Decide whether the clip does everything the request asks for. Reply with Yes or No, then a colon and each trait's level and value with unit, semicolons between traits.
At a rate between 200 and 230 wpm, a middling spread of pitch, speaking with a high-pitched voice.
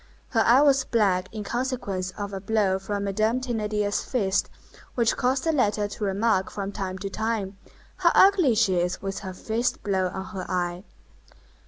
No: average, 175 wpm; average, 3.3 semitones; high, 205 Hz